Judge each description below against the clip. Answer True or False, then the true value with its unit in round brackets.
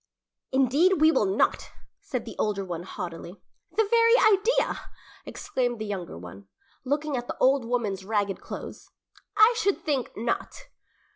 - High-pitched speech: True (245 Hz)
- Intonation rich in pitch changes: True (8.1 semitones)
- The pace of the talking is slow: False (145 wpm)